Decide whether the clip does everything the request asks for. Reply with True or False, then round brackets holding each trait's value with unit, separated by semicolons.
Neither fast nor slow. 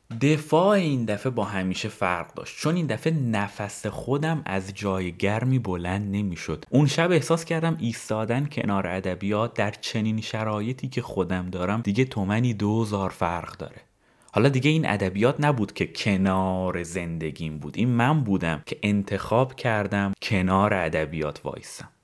True (145 wpm)